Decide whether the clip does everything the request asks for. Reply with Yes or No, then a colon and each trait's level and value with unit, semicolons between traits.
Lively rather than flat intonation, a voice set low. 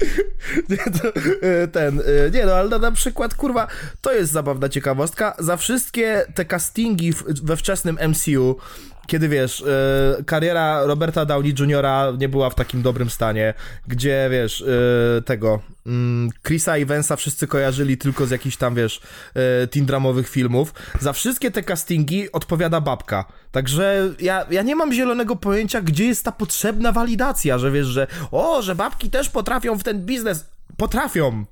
No: wide, 7.1 semitones; medium, 155 Hz